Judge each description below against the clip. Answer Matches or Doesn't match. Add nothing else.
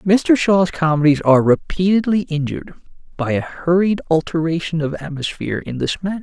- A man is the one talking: Matches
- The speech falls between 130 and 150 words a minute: Matches